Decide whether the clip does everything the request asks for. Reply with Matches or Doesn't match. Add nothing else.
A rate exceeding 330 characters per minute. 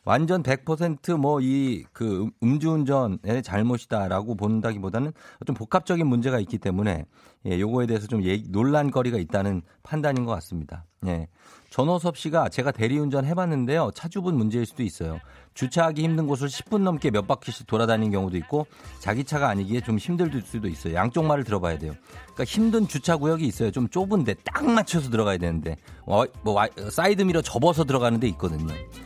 Matches